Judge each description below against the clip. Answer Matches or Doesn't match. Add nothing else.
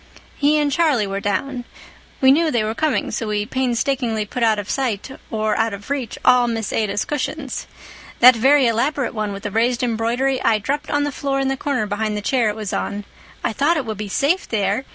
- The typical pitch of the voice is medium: Doesn't match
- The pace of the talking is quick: Matches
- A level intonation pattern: Doesn't match